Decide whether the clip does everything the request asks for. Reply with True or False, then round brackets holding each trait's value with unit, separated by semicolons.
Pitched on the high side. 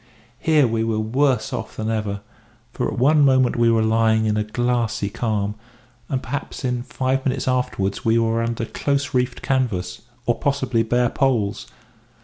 False (115 Hz)